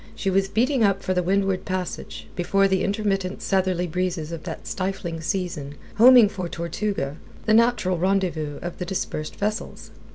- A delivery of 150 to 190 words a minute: Yes, average, 160 wpm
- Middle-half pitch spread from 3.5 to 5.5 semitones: No, narrow, 2.4 semitones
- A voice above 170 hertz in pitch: Yes, medium, 185 Hz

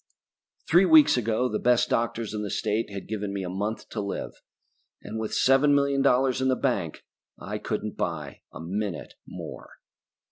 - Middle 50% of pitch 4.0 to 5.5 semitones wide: Yes, average, 4.3 semitones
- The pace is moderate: Yes, average, 175 wpm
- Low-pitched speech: Yes, low, 115 Hz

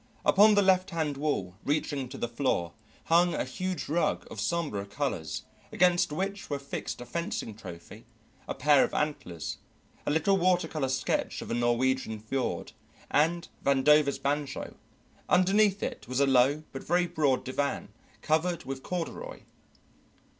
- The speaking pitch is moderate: Yes, medium, 145 Hz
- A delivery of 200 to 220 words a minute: No, average, 150 wpm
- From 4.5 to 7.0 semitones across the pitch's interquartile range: Yes, average, 4.9 semitones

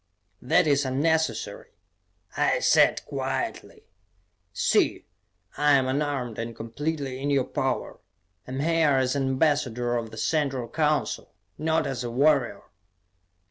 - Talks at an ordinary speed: No, slow, 130 wpm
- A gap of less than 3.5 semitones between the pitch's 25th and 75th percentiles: Yes, average, 2.9 semitones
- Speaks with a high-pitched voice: No, medium, 140 Hz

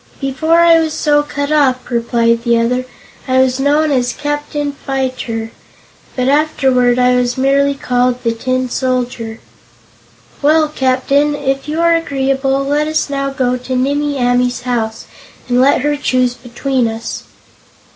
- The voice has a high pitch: Yes, very high, 265 Hz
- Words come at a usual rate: Yes, average, 145 wpm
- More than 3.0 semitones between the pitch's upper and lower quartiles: No, narrow, 2.6 semitones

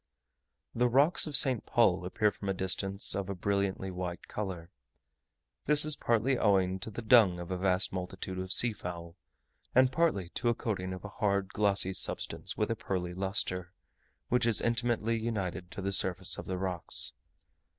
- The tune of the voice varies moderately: Yes, average, 3.8 semitones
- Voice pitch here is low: Yes, low, 100 Hz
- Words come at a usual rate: Yes, average, 170 wpm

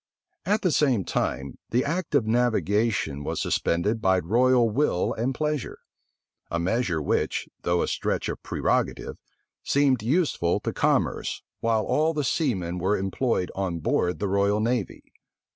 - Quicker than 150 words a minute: No, average, 145 wpm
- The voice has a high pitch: No, low, 110 Hz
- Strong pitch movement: Yes, wide, 6.1 semitones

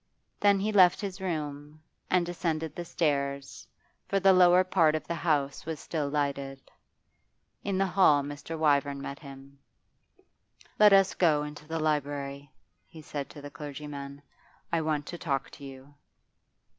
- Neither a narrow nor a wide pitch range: Yes, average, 3.6 semitones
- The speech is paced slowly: No, average, 155 wpm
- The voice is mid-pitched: Yes, medium, 150 Hz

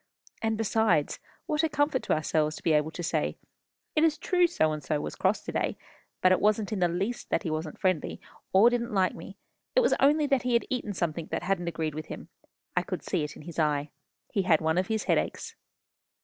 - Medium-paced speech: No, fast, 230 wpm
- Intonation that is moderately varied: No, wide, 6.9 semitones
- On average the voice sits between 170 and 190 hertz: Yes, medium, 185 Hz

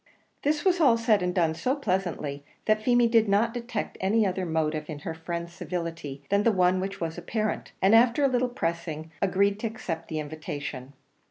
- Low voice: No, medium, 185 Hz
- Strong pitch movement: Yes, wide, 5.8 semitones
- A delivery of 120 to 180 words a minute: No, average, 190 wpm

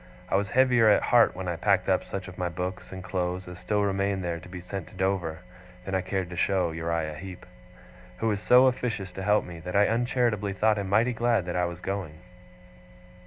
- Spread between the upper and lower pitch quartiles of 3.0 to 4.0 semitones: No, narrow, 2.6 semitones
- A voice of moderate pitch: No, very low, 95 Hz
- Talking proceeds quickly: Yes, fast, 225 wpm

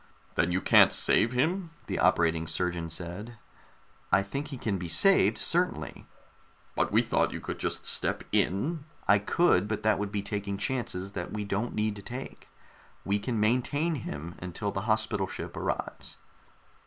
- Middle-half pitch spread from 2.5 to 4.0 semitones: No, average, 4.8 semitones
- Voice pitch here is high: No, low, 105 Hz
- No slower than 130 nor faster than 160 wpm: No, average, 170 wpm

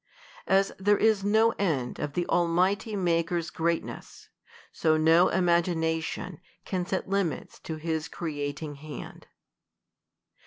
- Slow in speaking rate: Yes, slow, 120 wpm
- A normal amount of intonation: Yes, average, 3.0 semitones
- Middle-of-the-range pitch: Yes, medium, 170 Hz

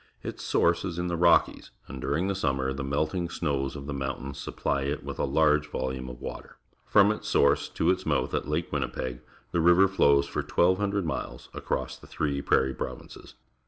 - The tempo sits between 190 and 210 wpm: Yes, average, 200 wpm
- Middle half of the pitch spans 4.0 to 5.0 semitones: Yes, average, 4.3 semitones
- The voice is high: No, very low, 75 Hz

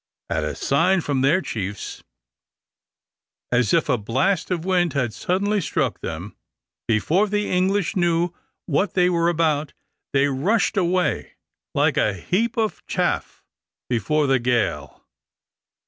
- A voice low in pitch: No, medium, 165 Hz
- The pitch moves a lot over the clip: Yes, wide, 6.8 semitones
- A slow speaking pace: Yes, slow, 130 wpm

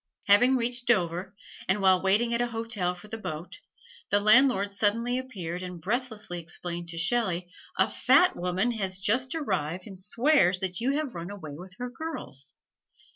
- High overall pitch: Yes, high, 200 Hz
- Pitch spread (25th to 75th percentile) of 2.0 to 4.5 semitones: No, average, 5.2 semitones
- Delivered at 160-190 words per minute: Yes, average, 170 wpm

